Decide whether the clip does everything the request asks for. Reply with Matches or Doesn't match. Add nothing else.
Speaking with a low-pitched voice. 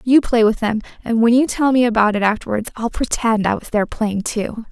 Doesn't match